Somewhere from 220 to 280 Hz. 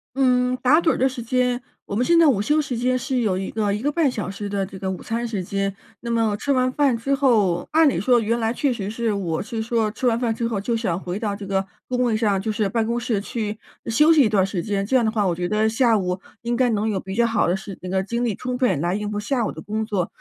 Yes: high, 225 Hz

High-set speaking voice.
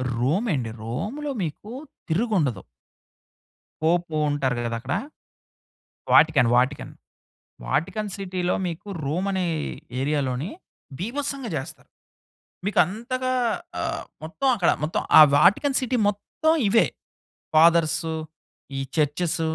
No: medium, 170 Hz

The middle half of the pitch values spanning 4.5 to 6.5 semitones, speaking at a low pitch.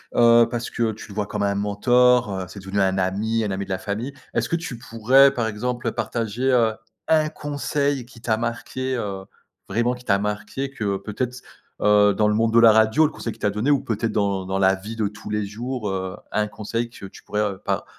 No: average, 3.2 semitones; low, 110 Hz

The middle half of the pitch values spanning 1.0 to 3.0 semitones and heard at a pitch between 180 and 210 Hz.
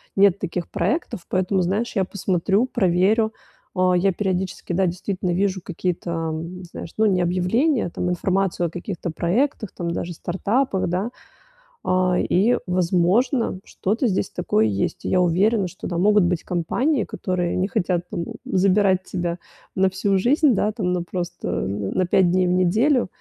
Yes: narrow, 2.4 semitones; medium, 185 Hz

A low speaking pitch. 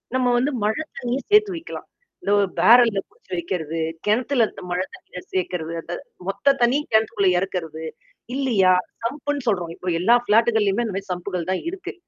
No: high, 210 Hz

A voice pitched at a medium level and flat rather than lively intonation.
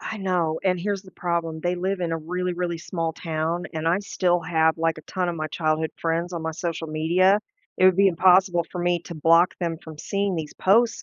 Yes: medium, 175 Hz; narrow, 2.2 semitones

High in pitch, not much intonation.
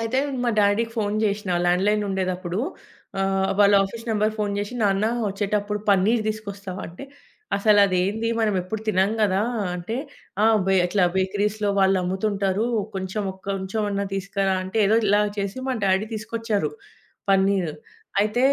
Yes: high, 200 Hz; narrow, 1.9 semitones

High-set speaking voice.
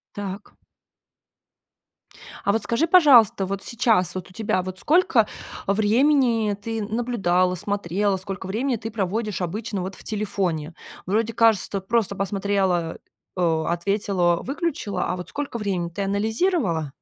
Yes: high, 200 Hz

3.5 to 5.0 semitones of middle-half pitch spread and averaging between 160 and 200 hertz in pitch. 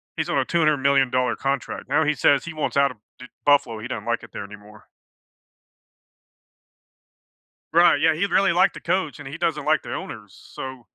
No: average, 3.9 semitones; medium, 140 Hz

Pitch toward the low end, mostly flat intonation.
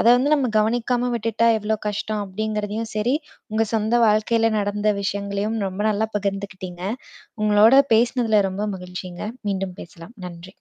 No: high, 210 Hz; narrow, 2.3 semitones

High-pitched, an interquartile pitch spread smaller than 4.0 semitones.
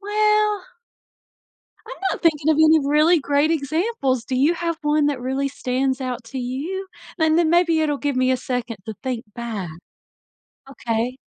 No: very high, 290 Hz; average, 4.4 semitones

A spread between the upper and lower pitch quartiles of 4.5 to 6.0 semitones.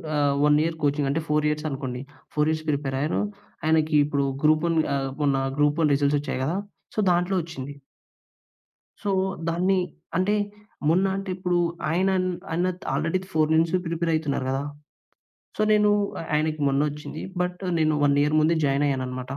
No: average, 2.9 semitones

